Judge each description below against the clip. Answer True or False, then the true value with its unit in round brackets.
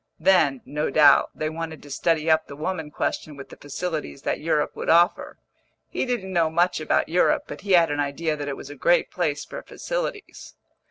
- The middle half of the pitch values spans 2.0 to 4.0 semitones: True (3.1 semitones)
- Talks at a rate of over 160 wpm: True (205 wpm)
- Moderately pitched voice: True (160 Hz)